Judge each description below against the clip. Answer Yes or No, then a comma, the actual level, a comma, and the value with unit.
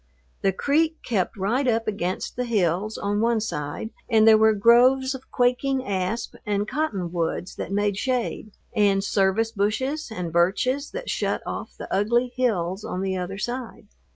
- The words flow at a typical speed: Yes, average, 160 wpm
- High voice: Yes, high, 220 Hz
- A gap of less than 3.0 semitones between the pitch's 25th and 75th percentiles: No, average, 4.3 semitones